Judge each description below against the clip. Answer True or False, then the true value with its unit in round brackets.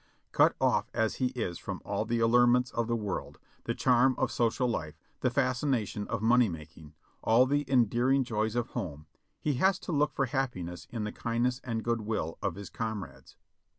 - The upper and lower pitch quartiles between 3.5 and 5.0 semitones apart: False (3.1 semitones)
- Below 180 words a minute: False (185 wpm)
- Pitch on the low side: True (115 Hz)